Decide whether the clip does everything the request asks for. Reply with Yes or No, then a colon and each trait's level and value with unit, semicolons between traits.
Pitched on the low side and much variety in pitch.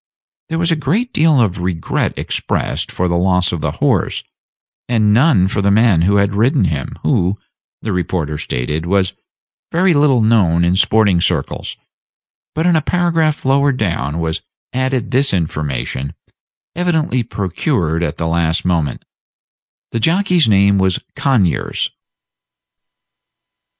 Yes: low, 100 Hz; wide, 8.2 semitones